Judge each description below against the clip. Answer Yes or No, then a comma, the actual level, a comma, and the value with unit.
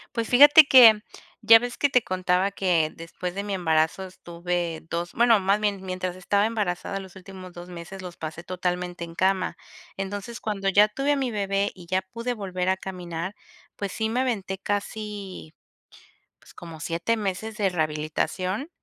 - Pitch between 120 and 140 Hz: No, high, 190 Hz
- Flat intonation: No, average, 3.0 semitones